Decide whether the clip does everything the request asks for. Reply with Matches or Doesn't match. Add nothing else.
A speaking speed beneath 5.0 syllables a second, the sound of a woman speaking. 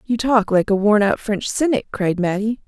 Matches